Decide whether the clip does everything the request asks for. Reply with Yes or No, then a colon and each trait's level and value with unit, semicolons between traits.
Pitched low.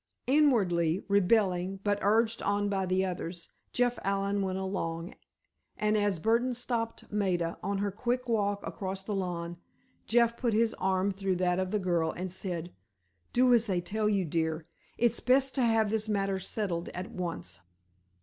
No: high, 195 Hz